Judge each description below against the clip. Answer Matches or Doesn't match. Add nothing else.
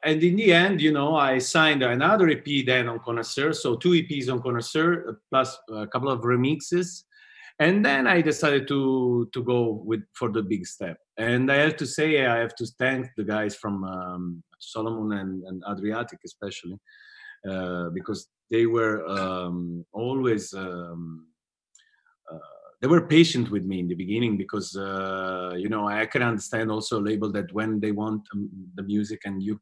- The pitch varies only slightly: Doesn't match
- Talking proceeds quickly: Doesn't match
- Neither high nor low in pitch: Doesn't match